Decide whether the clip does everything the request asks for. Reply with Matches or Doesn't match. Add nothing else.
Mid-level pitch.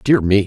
Doesn't match